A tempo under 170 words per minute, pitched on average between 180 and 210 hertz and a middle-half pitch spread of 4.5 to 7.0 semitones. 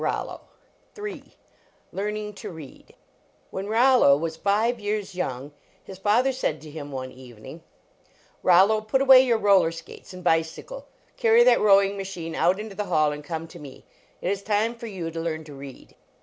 No: average, 175 wpm; high, 190 Hz; average, 5.1 semitones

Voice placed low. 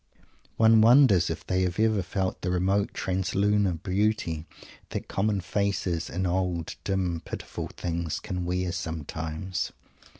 Yes: very low, 90 Hz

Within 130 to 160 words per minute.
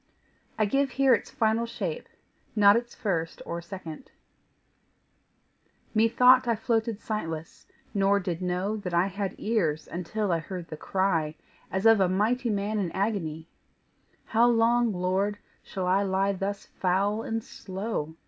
Yes: average, 145 wpm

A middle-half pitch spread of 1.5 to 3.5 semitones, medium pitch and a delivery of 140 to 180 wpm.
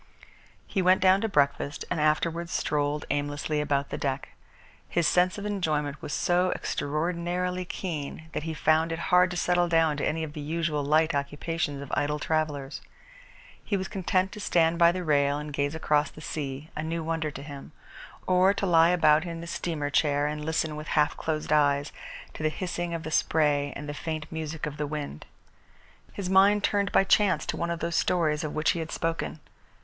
No: average, 2.8 semitones; medium, 160 Hz; average, 195 wpm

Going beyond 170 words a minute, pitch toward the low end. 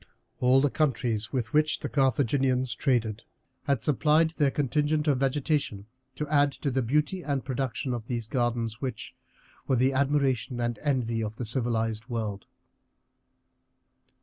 No: average, 145 wpm; low, 130 Hz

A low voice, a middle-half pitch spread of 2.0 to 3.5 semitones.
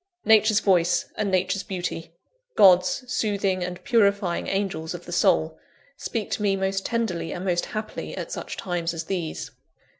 No: high, 190 Hz; average, 2.8 semitones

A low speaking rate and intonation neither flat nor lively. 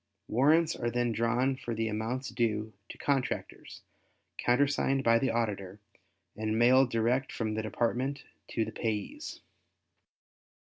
Yes: slow, 130 wpm; average, 3.0 semitones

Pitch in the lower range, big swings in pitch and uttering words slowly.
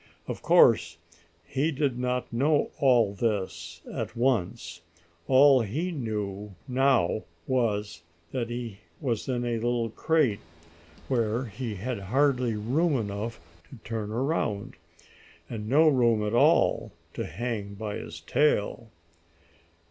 No: low, 115 Hz; average, 4.0 semitones; slow, 125 wpm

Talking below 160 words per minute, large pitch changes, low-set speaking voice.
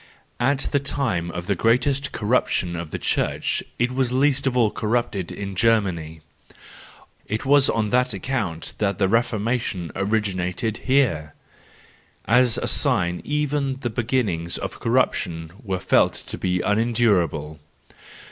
Yes: average, 140 wpm; wide, 5.8 semitones; low, 110 Hz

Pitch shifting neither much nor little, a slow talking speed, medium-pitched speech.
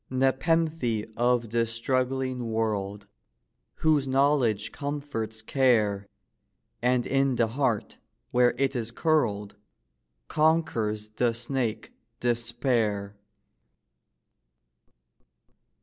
No: average, 3.5 semitones; slow, 80 wpm; low, 120 Hz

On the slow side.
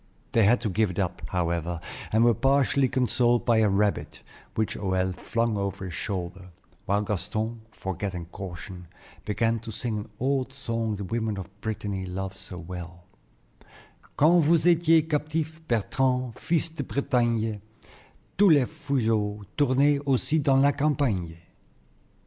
No: average, 145 wpm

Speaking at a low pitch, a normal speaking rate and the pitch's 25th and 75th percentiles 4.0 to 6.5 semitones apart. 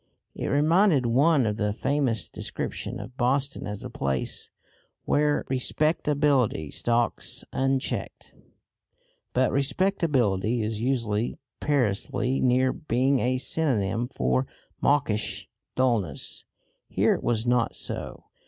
No: low, 125 Hz; slow, 105 wpm; average, 4.3 semitones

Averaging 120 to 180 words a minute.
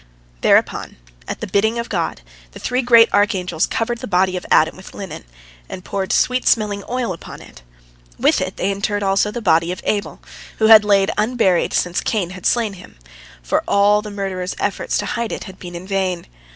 No: average, 200 wpm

